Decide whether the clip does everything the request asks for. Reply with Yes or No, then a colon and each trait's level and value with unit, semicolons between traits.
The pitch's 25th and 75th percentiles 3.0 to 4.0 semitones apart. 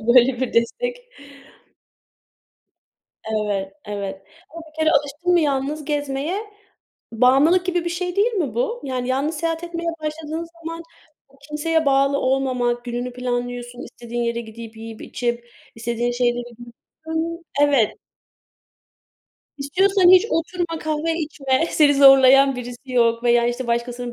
No: average, 5.0 semitones